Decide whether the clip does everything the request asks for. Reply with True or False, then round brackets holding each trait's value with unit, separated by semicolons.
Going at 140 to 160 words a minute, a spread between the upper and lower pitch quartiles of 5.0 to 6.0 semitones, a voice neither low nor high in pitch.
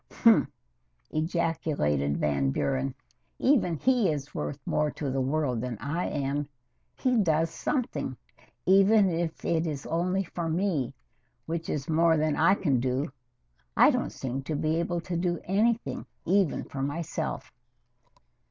False (145 wpm; 4.3 semitones; 160 Hz)